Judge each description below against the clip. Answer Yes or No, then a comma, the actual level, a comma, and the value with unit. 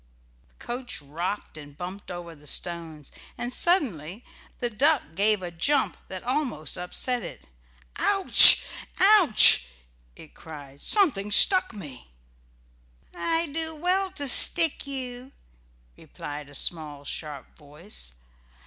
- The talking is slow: Yes, slow, 120 wpm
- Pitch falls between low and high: No, high, 205 Hz